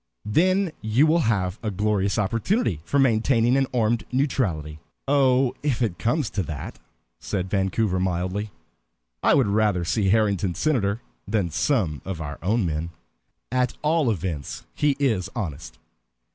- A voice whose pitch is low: Yes, low, 105 Hz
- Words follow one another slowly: No, average, 145 wpm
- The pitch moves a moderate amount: No, wide, 5.8 semitones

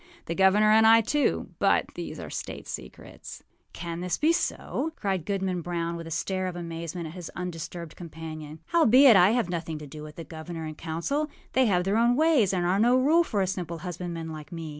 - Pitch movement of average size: Yes, average, 4.7 semitones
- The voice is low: No, medium, 180 Hz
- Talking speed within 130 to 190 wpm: No, fast, 205 wpm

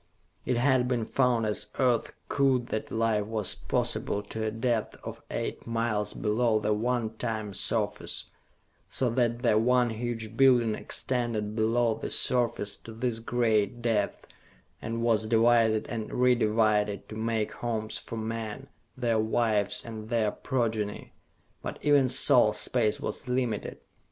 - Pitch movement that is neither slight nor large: No, narrow, 1.9 semitones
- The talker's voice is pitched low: Yes, low, 115 Hz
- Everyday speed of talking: Yes, average, 145 wpm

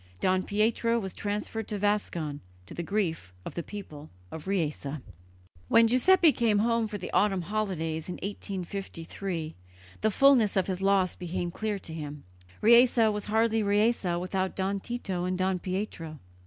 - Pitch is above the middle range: Yes, high, 195 Hz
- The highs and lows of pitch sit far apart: No, average, 3.6 semitones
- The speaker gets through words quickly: No, average, 155 wpm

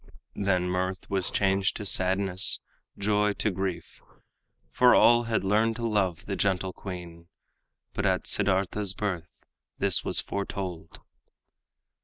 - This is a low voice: Yes, very low, 95 Hz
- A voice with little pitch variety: Yes, narrow, 2.1 semitones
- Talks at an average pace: No, slow, 125 wpm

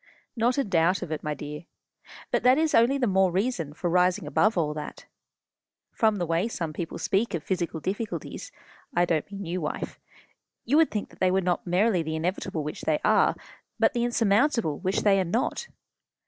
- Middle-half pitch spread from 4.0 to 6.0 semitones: Yes, average, 5.2 semitones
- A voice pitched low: No, medium, 185 Hz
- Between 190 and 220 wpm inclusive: Yes, average, 195 wpm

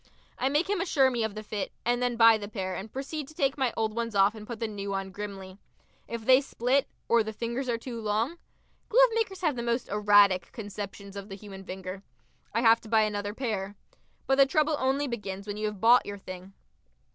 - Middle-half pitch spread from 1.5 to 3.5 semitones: No, average, 4.2 semitones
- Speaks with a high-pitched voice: Yes, high, 225 Hz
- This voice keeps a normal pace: No, fast, 220 wpm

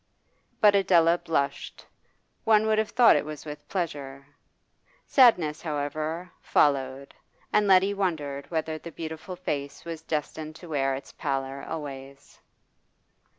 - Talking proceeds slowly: Yes, slow, 125 wpm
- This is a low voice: No, medium, 155 Hz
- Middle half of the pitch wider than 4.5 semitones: No, average, 4.1 semitones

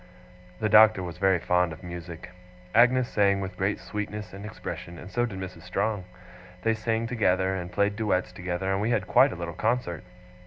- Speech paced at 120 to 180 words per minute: No, average, 190 wpm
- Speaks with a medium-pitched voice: No, very low, 95 Hz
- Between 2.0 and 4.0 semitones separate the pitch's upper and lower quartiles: Yes, average, 3.3 semitones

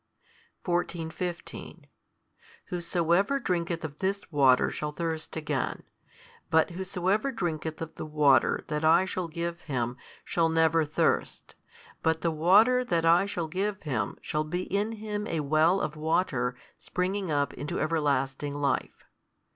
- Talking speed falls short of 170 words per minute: Yes, average, 140 wpm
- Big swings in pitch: No, average, 3.1 semitones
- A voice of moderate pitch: Yes, medium, 165 Hz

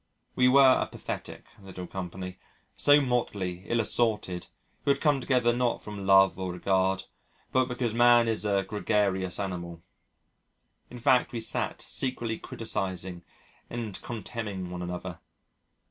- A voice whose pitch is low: Yes, low, 105 Hz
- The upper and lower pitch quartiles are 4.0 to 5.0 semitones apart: Yes, average, 4.4 semitones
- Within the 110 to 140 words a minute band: Yes, slow, 135 wpm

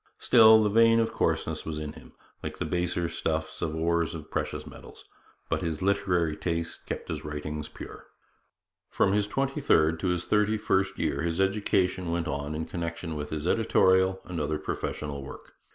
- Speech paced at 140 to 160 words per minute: No, average, 185 wpm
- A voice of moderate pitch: No, very low, 85 Hz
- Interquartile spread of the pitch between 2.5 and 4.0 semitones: Yes, average, 3.7 semitones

